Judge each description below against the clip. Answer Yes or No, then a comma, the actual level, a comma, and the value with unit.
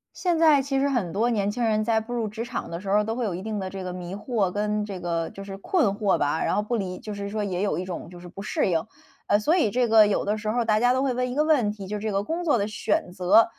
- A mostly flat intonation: No, average, 3.6 semitones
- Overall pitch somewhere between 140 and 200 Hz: No, high, 210 Hz